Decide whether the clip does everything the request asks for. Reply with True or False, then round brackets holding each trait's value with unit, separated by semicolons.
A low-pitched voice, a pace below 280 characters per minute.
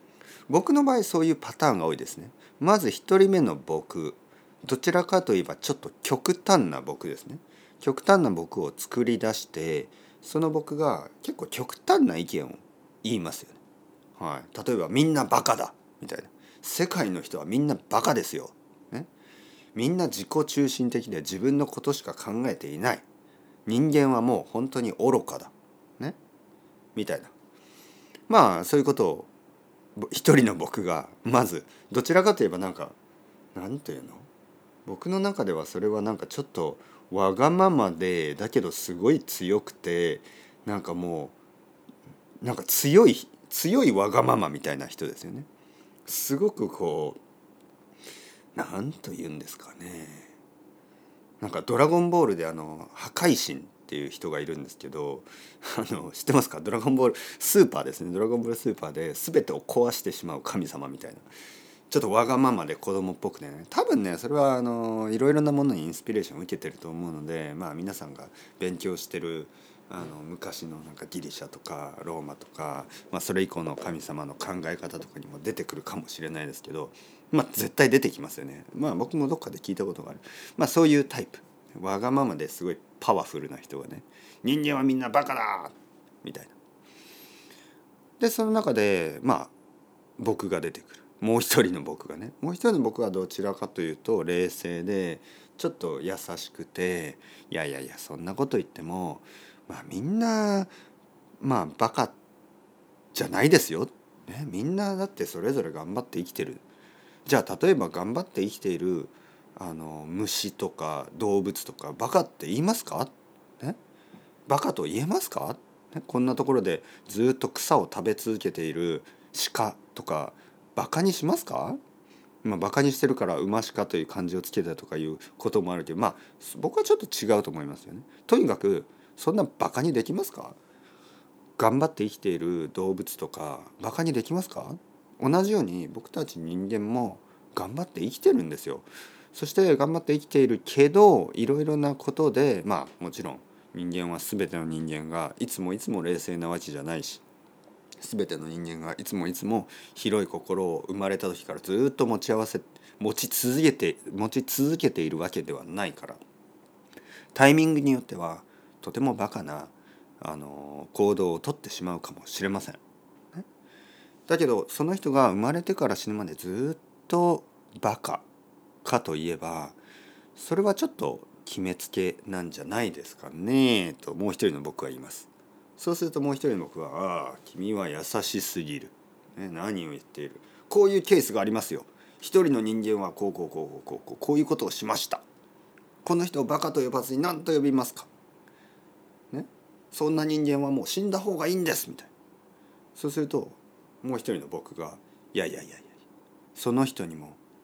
False (125 Hz; 330 characters per minute)